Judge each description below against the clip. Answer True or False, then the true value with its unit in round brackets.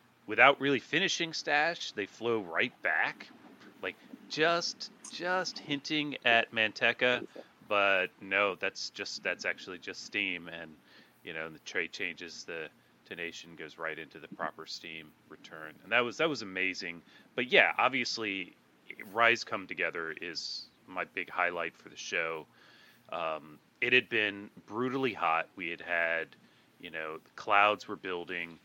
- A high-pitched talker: False (110 Hz)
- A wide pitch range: True (7.8 semitones)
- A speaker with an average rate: True (150 wpm)